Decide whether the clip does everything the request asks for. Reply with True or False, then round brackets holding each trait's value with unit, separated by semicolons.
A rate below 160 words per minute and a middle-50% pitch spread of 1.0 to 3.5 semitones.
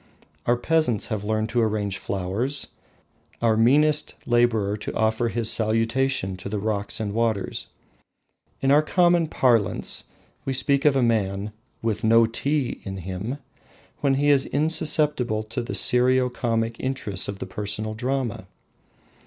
False (145 wpm; 3.9 semitones)